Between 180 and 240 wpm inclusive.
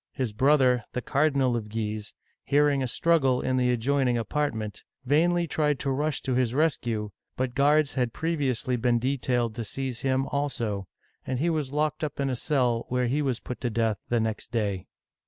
Yes: average, 185 wpm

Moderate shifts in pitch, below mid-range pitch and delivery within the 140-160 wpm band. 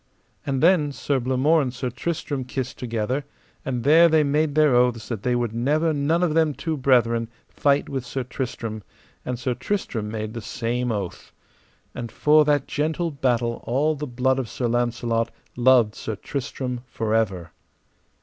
No: average, 3.8 semitones; low, 125 Hz; average, 170 wpm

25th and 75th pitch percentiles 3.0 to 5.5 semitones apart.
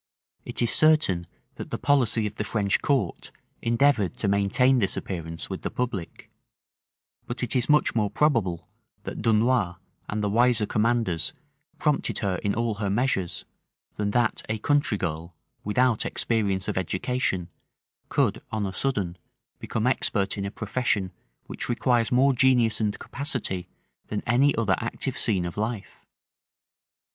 Yes: average, 4.3 semitones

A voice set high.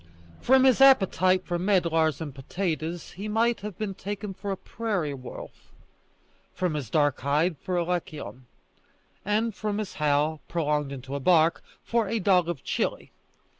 No: medium, 180 Hz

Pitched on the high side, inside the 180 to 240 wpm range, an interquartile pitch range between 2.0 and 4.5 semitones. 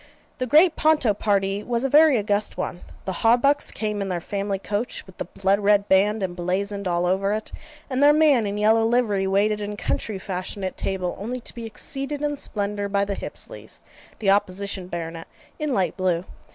Yes: high, 205 Hz; average, 190 wpm; average, 3.4 semitones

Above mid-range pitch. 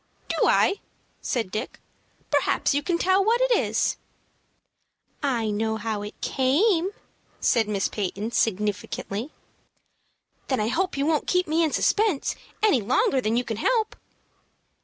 Yes: very high, 260 Hz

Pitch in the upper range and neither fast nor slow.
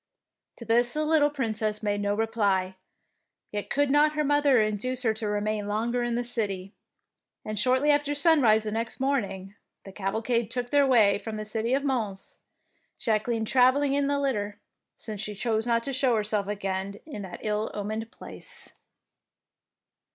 Yes: high, 225 Hz; average, 160 wpm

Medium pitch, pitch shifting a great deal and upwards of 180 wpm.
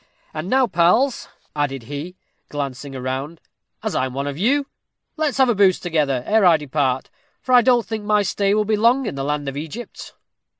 Yes: medium, 170 Hz; wide, 7.7 semitones; average, 200 wpm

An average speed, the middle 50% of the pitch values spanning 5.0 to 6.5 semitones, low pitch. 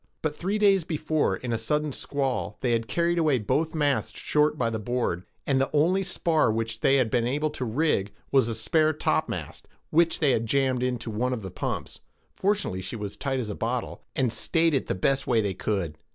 No: fast, 210 wpm; average, 5.3 semitones; low, 130 Hz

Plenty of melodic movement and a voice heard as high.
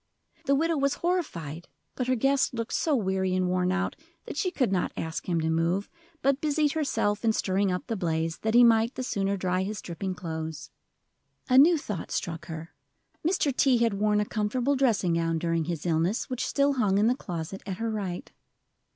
Yes: wide, 6.7 semitones; high, 205 Hz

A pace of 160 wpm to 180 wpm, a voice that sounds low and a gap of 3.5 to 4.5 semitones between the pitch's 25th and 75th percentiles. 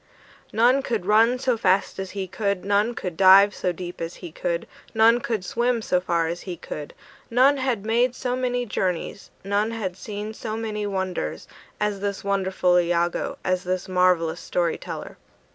No: average, 175 wpm; high, 200 Hz; average, 3.8 semitones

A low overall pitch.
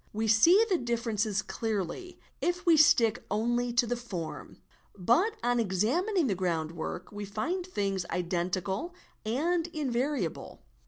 No: high, 230 Hz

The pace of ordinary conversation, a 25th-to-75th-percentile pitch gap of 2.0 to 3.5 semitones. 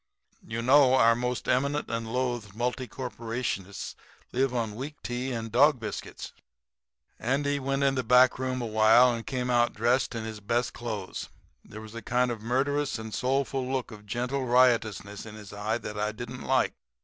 Yes: average, 175 wpm; narrow, 2.6 semitones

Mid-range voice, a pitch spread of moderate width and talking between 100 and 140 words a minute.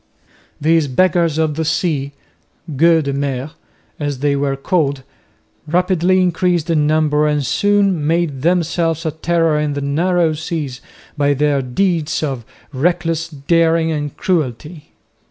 Yes: medium, 155 Hz; average, 3.0 semitones; slow, 135 wpm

